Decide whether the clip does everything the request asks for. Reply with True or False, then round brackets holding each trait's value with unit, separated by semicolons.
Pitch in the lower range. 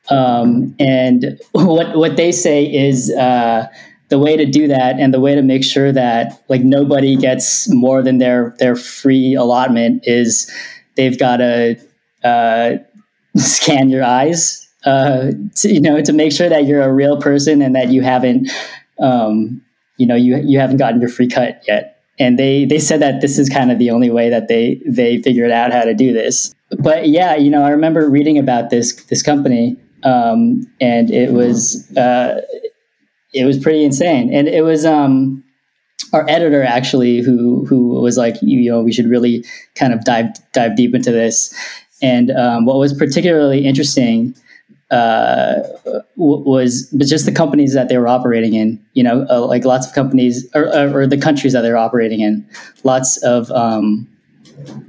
True (130 Hz)